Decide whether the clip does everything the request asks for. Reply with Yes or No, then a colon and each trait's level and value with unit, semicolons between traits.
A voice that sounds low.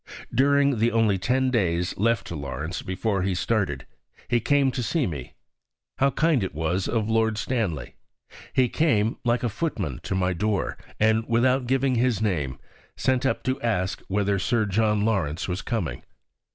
Yes: low, 110 Hz